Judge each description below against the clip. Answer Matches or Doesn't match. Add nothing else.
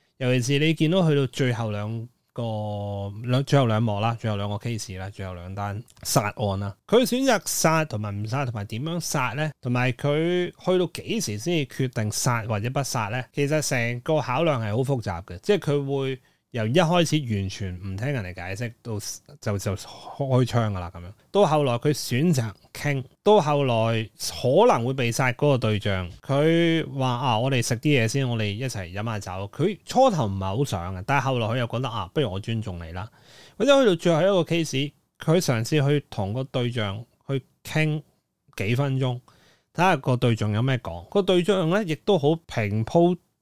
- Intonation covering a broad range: Matches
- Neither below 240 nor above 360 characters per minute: Matches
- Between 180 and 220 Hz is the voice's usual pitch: Doesn't match